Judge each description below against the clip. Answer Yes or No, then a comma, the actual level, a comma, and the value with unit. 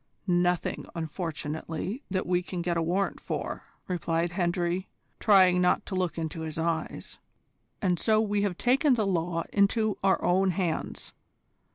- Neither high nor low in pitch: Yes, medium, 180 Hz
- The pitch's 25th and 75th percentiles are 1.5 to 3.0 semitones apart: Yes, average, 2.7 semitones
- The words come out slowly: No, average, 150 wpm